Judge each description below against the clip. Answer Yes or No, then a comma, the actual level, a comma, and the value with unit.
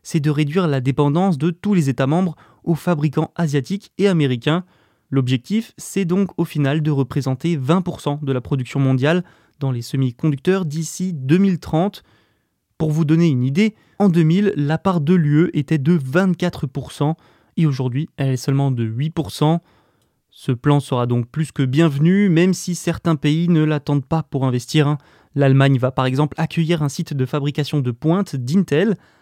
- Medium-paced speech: Yes, average, 165 wpm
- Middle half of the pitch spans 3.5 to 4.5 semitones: Yes, average, 3.8 semitones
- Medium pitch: Yes, medium, 155 Hz